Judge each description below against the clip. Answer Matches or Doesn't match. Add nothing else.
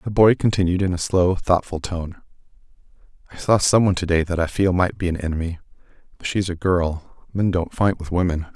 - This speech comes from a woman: Doesn't match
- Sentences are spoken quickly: Matches